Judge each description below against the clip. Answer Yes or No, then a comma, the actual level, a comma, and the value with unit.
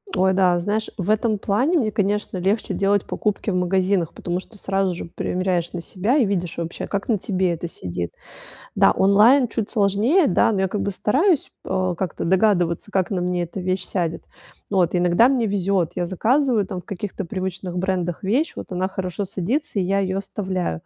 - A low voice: No, high, 190 Hz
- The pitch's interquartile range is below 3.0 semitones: Yes, narrow, 2.6 semitones